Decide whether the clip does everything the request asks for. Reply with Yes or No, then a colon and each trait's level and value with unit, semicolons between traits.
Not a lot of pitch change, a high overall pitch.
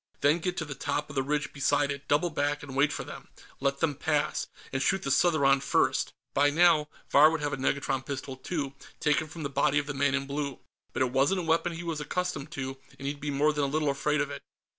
No: narrow, 1.7 semitones; medium, 145 Hz